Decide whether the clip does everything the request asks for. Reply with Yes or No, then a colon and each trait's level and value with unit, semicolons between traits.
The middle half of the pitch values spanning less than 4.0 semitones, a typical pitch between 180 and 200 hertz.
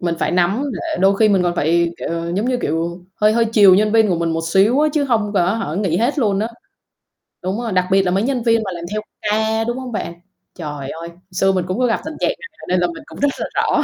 No: average, 4.6 semitones; high, 195 Hz